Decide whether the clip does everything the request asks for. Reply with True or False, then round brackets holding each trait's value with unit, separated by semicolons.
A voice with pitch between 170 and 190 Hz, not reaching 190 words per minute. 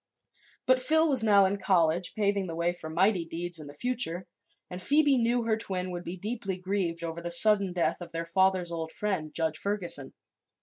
False (185 Hz; 200 wpm)